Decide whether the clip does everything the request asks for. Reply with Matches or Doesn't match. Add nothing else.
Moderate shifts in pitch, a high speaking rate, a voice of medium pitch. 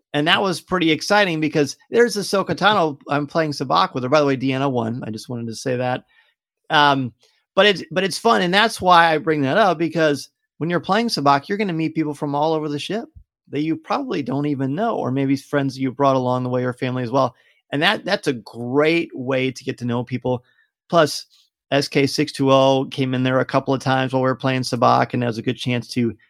Matches